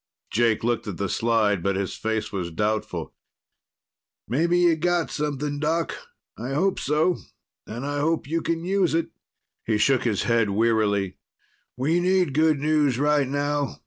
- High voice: No, medium, 140 Hz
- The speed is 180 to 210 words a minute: No, average, 155 wpm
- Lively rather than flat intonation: Yes, wide, 6.4 semitones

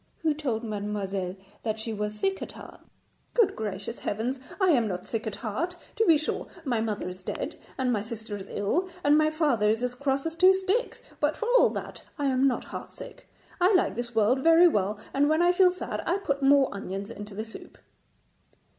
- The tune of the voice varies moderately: No, wide, 7.3 semitones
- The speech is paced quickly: Yes, fast, 210 wpm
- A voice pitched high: Yes, very high, 250 Hz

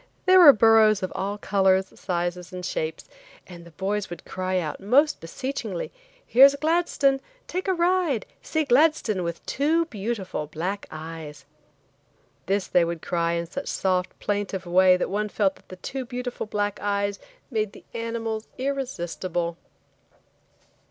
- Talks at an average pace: Yes, average, 145 wpm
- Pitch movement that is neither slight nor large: No, wide, 6.1 semitones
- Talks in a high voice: Yes, high, 205 Hz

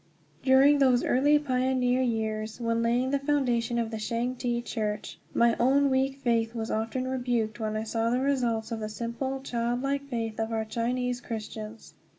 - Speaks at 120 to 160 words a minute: No, average, 170 wpm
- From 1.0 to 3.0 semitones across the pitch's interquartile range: Yes, narrow, 2.5 semitones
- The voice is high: Yes, high, 240 Hz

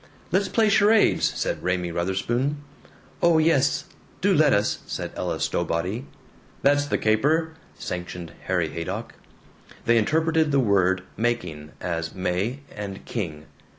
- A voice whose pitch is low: Yes, low, 110 Hz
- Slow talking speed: Yes, slow, 125 wpm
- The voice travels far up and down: Yes, wide, 8.7 semitones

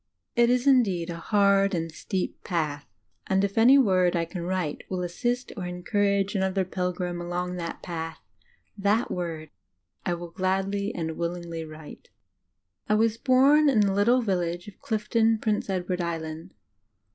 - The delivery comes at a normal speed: Yes, average, 150 wpm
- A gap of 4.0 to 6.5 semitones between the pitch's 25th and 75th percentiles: No, average, 3.4 semitones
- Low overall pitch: No, medium, 185 Hz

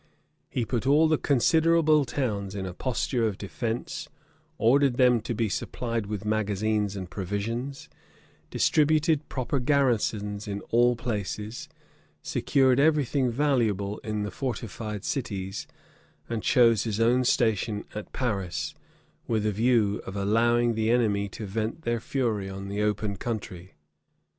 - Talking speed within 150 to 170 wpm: No, average, 140 wpm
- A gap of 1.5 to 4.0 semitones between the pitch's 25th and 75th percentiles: Yes, average, 3.6 semitones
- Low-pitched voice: Yes, low, 115 Hz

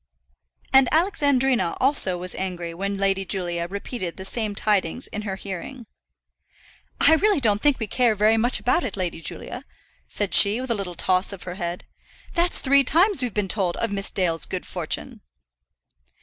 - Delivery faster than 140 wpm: Yes, average, 175 wpm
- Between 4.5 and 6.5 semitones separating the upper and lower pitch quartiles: Yes, wide, 5.5 semitones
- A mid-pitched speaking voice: No, high, 205 Hz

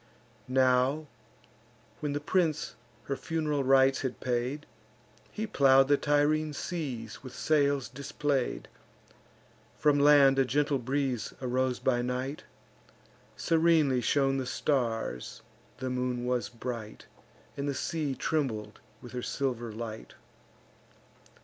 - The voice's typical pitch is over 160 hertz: No, low, 135 Hz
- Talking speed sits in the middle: No, slow, 115 wpm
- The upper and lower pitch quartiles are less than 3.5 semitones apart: Yes, narrow, 2.6 semitones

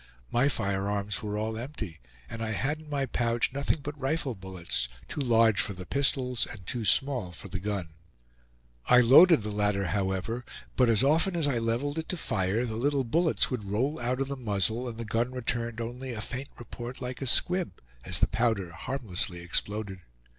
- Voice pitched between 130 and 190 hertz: No, low, 115 Hz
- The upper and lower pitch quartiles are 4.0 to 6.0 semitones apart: Yes, average, 4.7 semitones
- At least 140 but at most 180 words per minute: No, average, 190 wpm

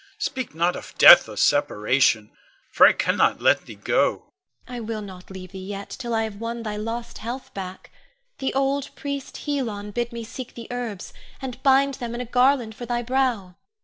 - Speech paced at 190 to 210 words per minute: Yes, average, 195 wpm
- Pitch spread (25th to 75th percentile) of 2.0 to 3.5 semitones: No, average, 4.1 semitones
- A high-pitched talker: Yes, high, 235 Hz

